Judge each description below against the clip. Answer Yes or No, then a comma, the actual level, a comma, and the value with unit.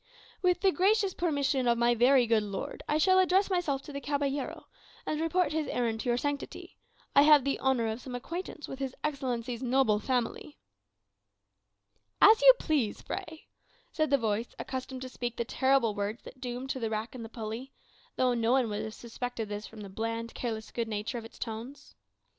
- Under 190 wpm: No, average, 195 wpm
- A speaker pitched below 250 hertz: No, very high, 255 Hz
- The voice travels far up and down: No, average, 4.0 semitones